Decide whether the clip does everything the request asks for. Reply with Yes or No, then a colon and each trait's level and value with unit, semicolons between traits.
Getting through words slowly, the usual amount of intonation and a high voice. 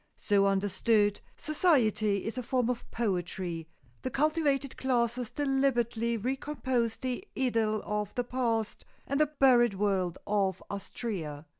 Yes: slow, 125 wpm; average, 4.3 semitones; high, 235 Hz